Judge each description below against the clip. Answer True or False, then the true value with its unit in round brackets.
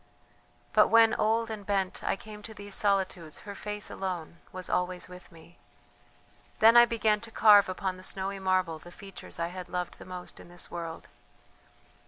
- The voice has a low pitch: False (190 Hz)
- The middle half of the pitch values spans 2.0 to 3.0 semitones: True (2.7 semitones)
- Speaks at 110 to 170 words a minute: False (180 wpm)